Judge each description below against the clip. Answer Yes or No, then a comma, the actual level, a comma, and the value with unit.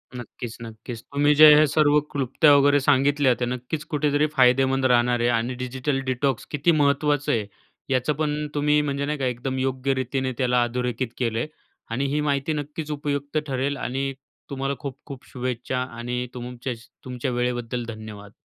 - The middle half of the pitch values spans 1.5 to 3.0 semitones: Yes, average, 2.7 semitones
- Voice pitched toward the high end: No, low, 130 Hz